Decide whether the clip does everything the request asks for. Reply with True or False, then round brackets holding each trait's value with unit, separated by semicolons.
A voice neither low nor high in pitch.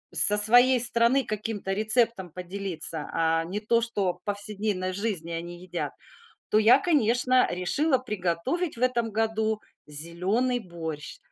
False (210 Hz)